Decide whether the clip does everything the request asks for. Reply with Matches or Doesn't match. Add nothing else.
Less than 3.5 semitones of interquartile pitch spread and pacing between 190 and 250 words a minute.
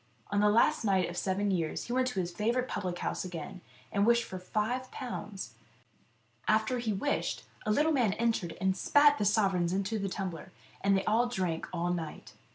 Doesn't match